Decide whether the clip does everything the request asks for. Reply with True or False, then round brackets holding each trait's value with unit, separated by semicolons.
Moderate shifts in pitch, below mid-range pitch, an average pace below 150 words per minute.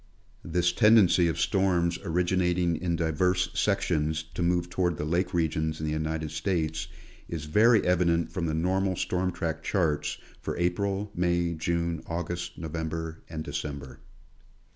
False (2.2 semitones; 85 Hz; 140 wpm)